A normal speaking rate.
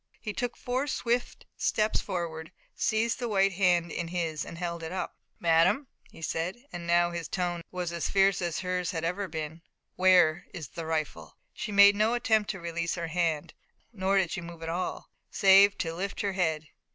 Yes: average, 190 wpm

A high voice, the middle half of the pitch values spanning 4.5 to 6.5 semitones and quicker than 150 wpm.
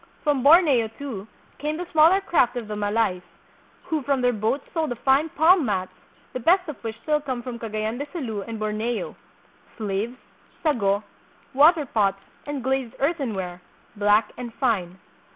Yes: high, 245 Hz; wide, 5.4 semitones; average, 160 wpm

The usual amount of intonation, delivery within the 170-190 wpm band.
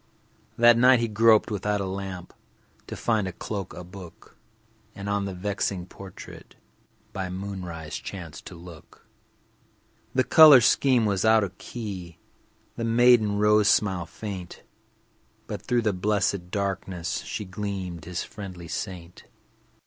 No: average, 3.0 semitones; slow, 135 wpm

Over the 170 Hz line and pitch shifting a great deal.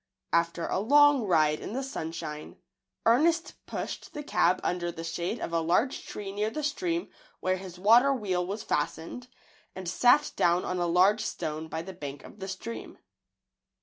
Yes: high, 190 Hz; wide, 6.4 semitones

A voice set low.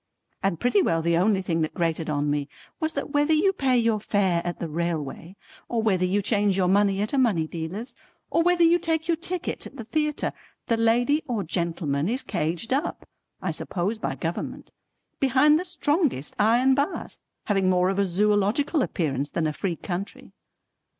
No: high, 205 Hz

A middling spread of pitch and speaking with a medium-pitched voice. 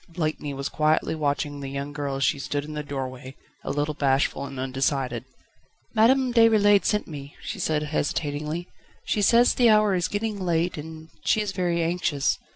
Yes: average, 4.7 semitones; medium, 155 Hz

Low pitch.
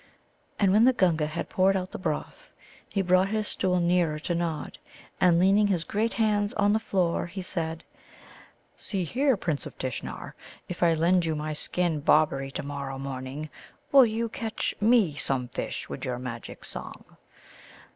No: medium, 175 Hz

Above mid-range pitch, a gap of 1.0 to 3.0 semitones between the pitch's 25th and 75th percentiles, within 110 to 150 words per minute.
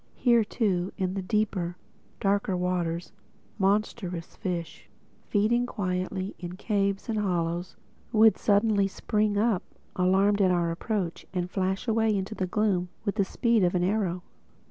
Yes: high, 195 Hz; average, 2.7 semitones; average, 145 wpm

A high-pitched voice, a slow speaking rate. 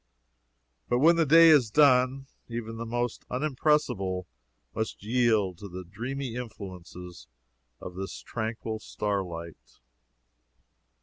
No: low, 115 Hz; slow, 110 wpm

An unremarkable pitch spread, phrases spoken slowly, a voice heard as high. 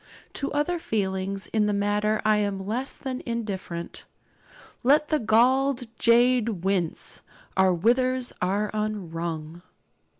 Yes: average, 4.6 semitones; slow, 120 wpm; high, 215 Hz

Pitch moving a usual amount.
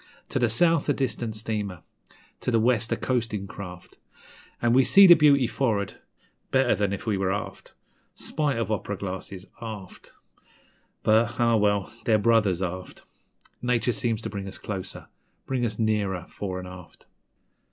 Yes: average, 3.4 semitones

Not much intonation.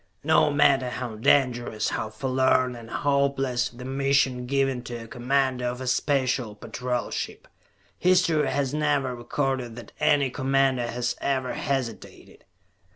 Yes: narrow, 2.2 semitones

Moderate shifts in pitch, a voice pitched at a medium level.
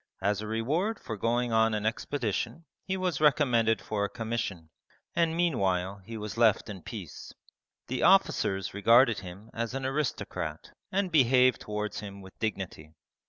No: average, 4.7 semitones; low, 115 Hz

